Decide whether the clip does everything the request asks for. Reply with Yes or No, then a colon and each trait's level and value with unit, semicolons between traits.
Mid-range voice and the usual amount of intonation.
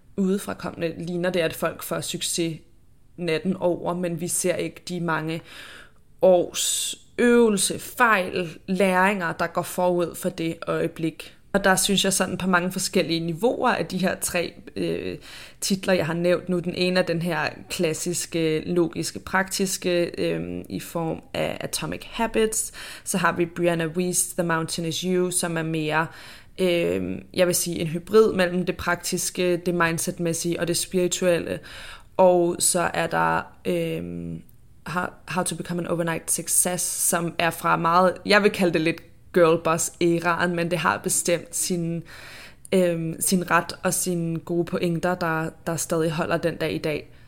No: medium, 175 Hz; narrow, 1.7 semitones